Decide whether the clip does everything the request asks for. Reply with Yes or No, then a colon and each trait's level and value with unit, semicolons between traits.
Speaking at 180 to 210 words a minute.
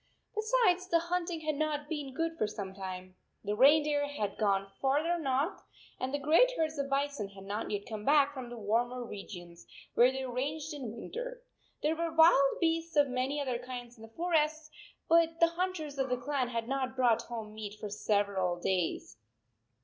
Yes: average, 190 wpm